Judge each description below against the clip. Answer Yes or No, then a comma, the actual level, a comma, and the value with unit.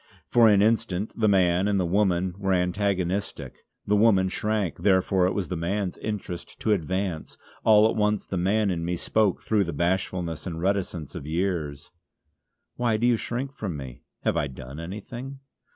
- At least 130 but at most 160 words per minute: No, average, 175 wpm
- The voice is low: Yes, very low, 95 Hz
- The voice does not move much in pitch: No, average, 3.3 semitones